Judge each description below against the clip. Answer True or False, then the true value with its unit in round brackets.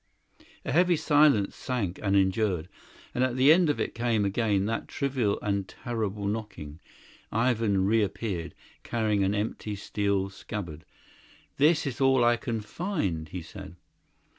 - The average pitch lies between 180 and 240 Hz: False (105 Hz)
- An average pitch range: True (4.2 semitones)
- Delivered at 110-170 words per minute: True (140 wpm)